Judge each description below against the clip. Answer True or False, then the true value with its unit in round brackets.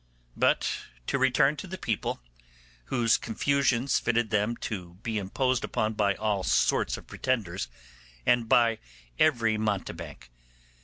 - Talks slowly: True (125 wpm)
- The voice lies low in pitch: True (115 Hz)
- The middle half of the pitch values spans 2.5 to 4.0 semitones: True (3.5 semitones)